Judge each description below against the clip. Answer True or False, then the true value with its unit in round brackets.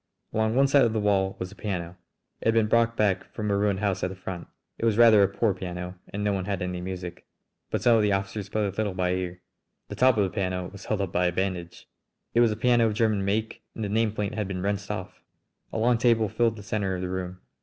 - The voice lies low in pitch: True (100 Hz)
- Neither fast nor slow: False (260 wpm)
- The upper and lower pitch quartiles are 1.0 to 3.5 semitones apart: True (3.0 semitones)